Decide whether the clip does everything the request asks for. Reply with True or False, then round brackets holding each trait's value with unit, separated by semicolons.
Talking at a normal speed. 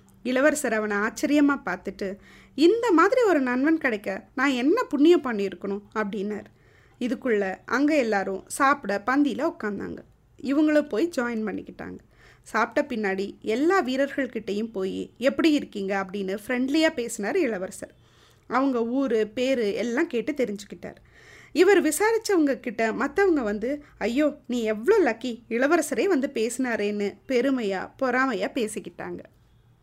True (110 wpm)